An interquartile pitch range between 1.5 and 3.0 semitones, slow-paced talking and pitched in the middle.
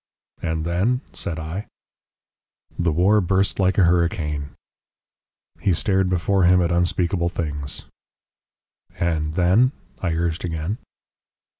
No: narrow, 2.6 semitones; slow, 115 wpm; very low, 85 Hz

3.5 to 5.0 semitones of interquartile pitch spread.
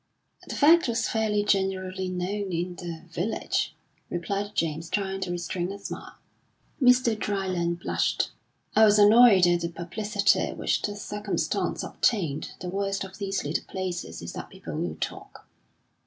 No: average, 2.9 semitones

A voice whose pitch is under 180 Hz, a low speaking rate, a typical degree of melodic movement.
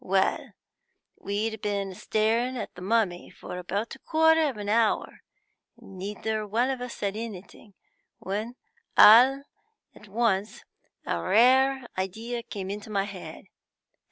No: high, 215 Hz; slow, 130 wpm; average, 3.3 semitones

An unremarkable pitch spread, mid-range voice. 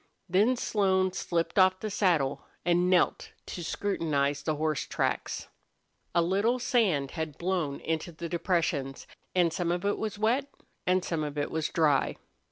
Yes: average, 3.3 semitones; medium, 175 Hz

